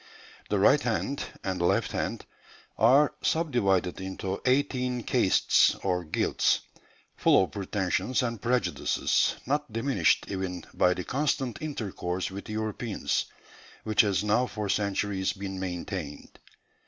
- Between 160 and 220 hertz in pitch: No, low, 105 Hz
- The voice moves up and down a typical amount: Yes, average, 4.8 semitones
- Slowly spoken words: Yes, slow, 120 wpm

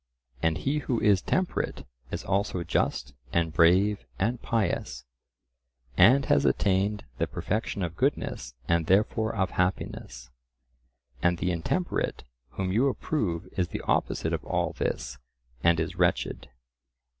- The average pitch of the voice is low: Yes, very low, 95 Hz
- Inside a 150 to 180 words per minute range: No, slow, 135 wpm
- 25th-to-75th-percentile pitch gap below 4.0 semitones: No, average, 4.5 semitones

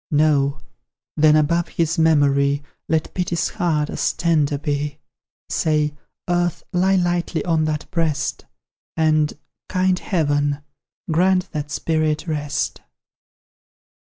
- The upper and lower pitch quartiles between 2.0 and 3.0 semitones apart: Yes, narrow, 2.6 semitones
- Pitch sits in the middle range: Yes, medium, 155 Hz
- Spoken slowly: Yes, slow, 105 wpm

